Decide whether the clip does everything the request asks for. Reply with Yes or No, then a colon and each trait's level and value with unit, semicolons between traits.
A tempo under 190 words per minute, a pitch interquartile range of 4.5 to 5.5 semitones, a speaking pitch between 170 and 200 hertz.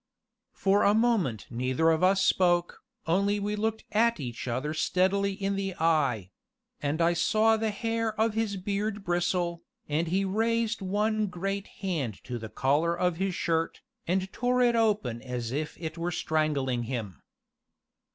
Yes: average, 160 wpm; average, 5.2 semitones; medium, 185 Hz